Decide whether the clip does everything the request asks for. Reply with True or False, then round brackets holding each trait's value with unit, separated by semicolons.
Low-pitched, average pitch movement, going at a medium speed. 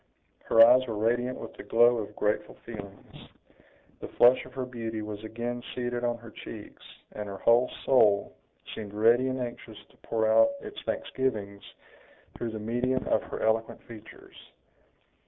False (115 Hz; 2.2 semitones; 160 wpm)